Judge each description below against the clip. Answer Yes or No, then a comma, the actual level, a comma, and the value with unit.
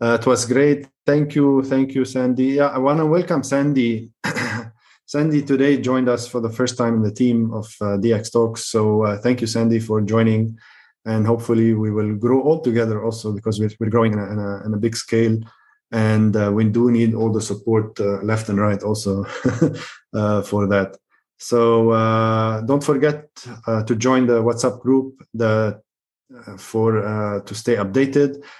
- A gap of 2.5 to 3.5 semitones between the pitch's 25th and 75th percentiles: Yes, average, 2.9 semitones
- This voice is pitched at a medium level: No, low, 115 Hz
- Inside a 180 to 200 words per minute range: Yes, average, 185 wpm